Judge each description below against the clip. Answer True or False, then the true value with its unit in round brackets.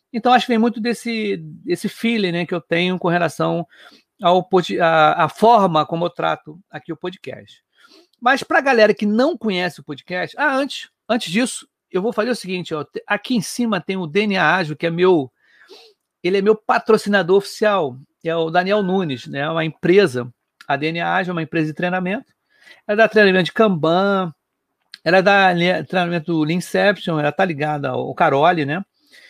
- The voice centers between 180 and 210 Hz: True (185 Hz)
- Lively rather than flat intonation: False (4.2 semitones)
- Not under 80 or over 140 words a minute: False (185 wpm)